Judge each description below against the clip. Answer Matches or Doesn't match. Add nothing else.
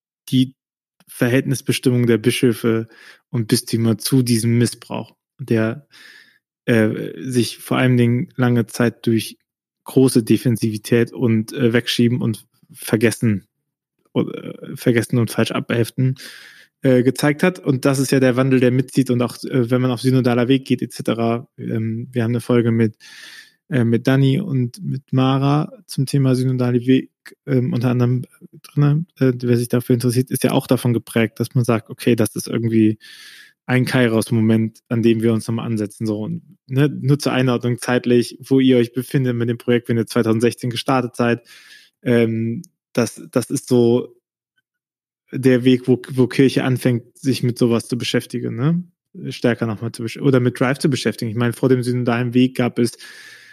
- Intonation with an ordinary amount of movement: Doesn't match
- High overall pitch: Doesn't match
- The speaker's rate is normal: Matches